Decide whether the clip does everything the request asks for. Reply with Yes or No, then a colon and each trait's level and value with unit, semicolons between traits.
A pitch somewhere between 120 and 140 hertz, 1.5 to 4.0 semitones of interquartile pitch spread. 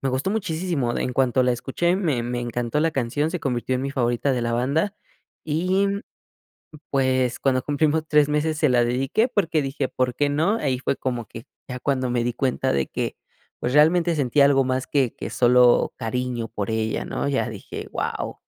Yes: low, 135 Hz; average, 3.7 semitones